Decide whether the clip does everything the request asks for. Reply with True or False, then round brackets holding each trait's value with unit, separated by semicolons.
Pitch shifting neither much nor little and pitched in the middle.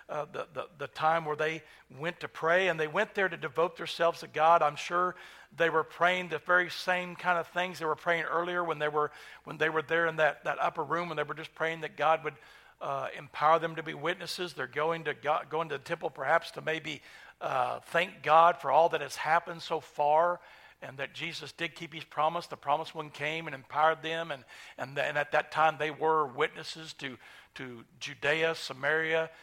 False (1.8 semitones; 160 Hz)